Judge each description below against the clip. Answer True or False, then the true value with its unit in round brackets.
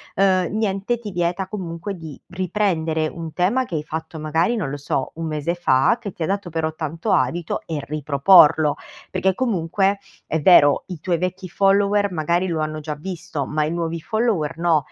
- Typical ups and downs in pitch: True (3.5 semitones)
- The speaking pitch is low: False (170 Hz)